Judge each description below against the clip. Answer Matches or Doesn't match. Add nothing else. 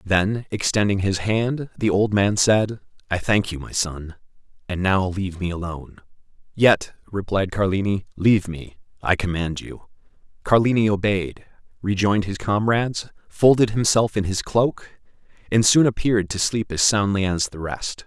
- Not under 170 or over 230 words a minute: Doesn't match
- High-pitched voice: Doesn't match